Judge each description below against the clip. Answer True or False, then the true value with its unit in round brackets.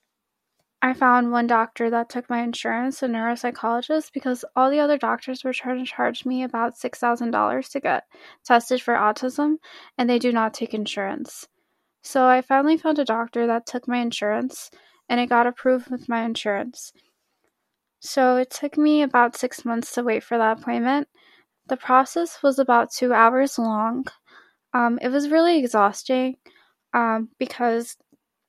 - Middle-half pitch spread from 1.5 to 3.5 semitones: True (2.9 semitones)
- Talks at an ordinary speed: True (160 wpm)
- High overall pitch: True (250 Hz)